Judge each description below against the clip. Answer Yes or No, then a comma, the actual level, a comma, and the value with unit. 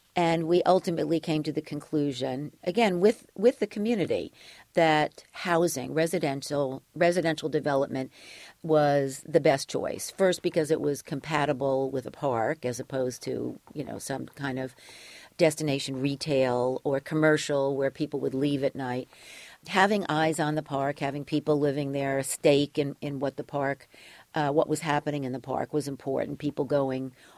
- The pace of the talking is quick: No, average, 160 wpm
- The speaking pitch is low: No, medium, 145 Hz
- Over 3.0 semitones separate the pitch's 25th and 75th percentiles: No, narrow, 2.6 semitones